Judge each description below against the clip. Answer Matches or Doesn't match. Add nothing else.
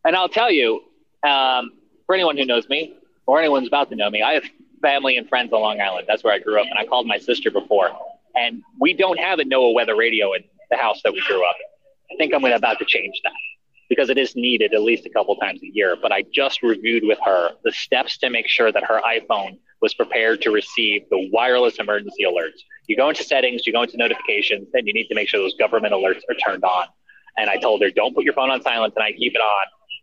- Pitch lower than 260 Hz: Doesn't match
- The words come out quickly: Matches